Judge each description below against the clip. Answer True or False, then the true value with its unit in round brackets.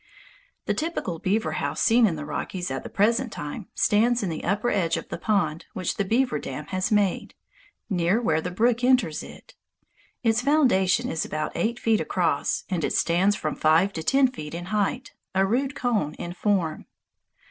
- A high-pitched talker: True (195 Hz)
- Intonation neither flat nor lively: False (5.7 semitones)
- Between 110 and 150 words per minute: False (185 wpm)